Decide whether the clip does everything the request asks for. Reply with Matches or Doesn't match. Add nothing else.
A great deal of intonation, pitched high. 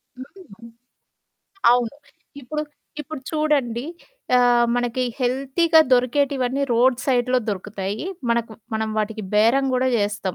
Doesn't match